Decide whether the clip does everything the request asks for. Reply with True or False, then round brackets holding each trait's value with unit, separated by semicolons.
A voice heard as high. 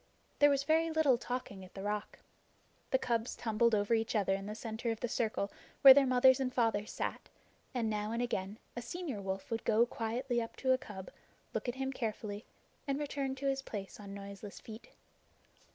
True (230 Hz)